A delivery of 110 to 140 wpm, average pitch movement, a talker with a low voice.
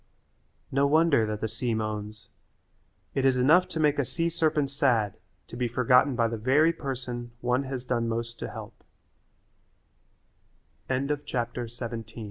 Yes: slow, 135 wpm; average, 3.3 semitones; low, 125 Hz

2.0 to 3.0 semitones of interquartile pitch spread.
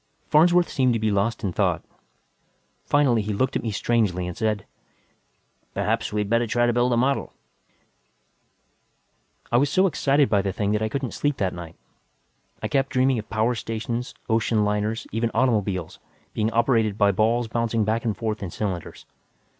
Yes: average, 2.7 semitones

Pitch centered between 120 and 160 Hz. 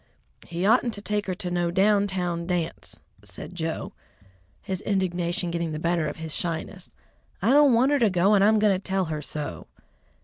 No: medium, 185 Hz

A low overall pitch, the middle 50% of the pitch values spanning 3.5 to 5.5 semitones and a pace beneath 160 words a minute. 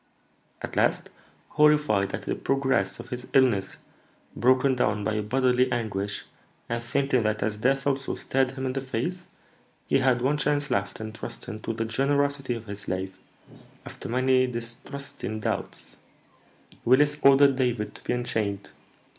Yes: low, 125 Hz; average, 3.9 semitones; average, 150 wpm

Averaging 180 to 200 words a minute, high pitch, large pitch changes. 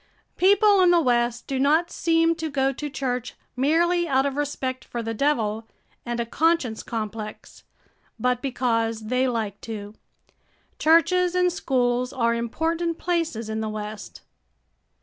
No: average, 145 wpm; very high, 260 Hz; wide, 6.2 semitones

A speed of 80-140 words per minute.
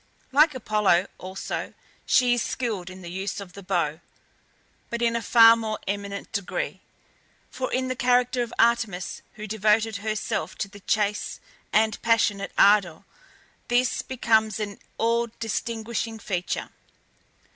Yes: slow, 135 wpm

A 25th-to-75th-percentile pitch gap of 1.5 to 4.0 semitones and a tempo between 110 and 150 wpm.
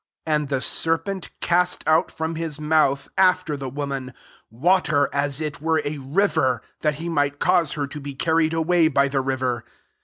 No: average, 2.8 semitones; average, 185 wpm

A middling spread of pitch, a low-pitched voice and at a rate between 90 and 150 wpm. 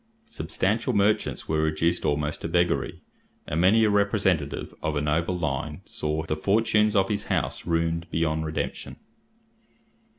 Yes: average, 4.5 semitones; very low, 85 Hz; average, 140 wpm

